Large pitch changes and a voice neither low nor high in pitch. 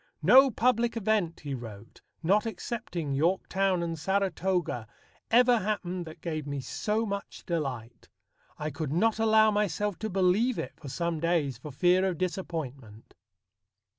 Yes: wide, 5.7 semitones; medium, 180 Hz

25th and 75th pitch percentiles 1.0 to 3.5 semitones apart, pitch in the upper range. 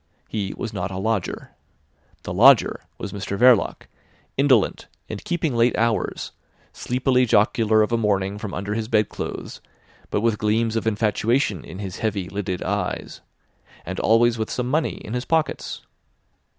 No: average, 2.8 semitones; low, 110 Hz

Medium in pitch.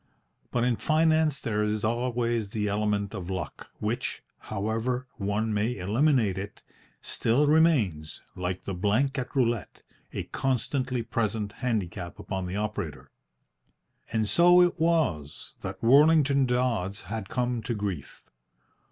No: low, 115 Hz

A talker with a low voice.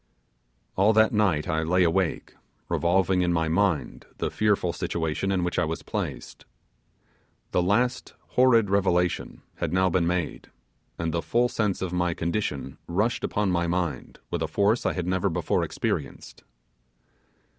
Yes: very low, 90 Hz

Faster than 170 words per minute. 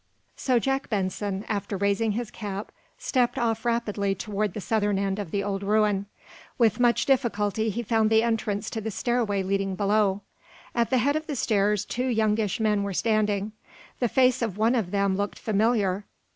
Yes: average, 180 wpm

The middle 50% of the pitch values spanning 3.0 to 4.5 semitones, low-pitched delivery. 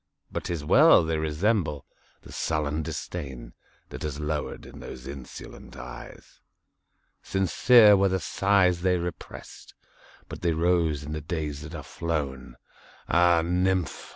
Yes: average, 3.4 semitones; very low, 80 Hz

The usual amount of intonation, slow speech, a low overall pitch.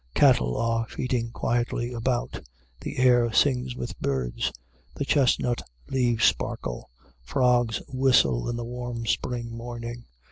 No: narrow, 1.3 semitones; slow, 120 wpm; low, 120 Hz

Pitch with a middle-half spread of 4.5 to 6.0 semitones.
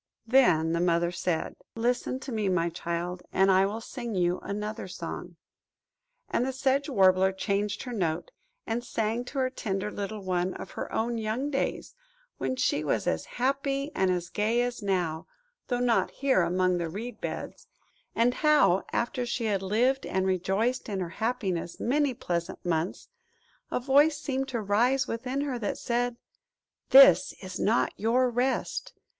Yes: average, 5.3 semitones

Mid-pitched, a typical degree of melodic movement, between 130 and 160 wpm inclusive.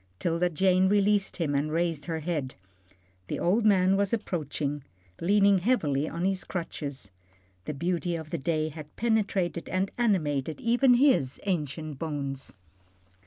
Yes: medium, 170 Hz; average, 4.5 semitones; average, 140 wpm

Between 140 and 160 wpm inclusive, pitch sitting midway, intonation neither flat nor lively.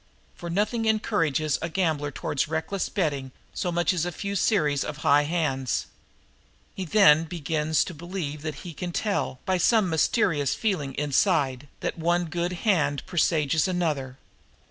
Yes: average, 150 wpm; medium, 165 Hz; average, 3.7 semitones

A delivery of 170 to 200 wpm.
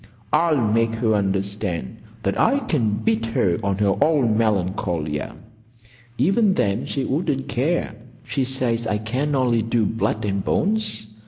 No: average, 145 wpm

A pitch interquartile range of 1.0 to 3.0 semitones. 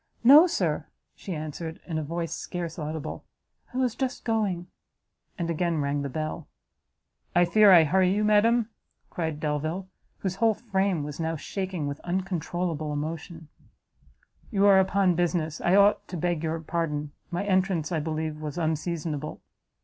No: average, 3.5 semitones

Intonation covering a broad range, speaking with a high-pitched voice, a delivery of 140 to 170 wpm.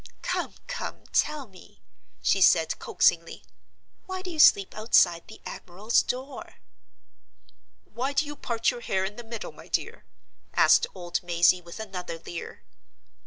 Yes: wide, 7.6 semitones; high, 220 Hz; average, 145 wpm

